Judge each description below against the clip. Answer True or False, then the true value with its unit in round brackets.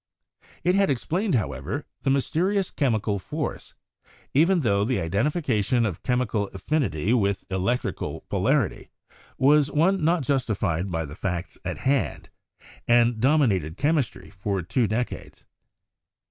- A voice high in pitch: False (120 Hz)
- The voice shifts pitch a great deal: True (6.9 semitones)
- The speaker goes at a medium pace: False (125 wpm)